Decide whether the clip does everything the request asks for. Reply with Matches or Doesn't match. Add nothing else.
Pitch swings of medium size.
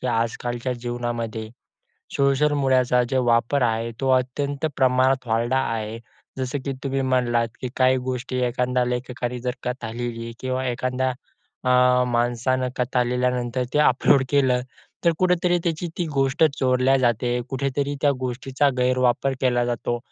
Doesn't match